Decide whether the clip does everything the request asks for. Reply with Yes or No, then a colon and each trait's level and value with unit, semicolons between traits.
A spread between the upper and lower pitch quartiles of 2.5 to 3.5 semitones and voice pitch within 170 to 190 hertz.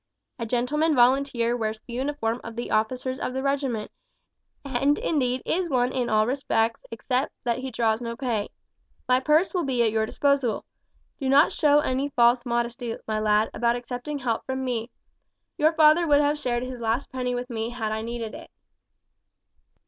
No: average, 3.0 semitones; very high, 250 Hz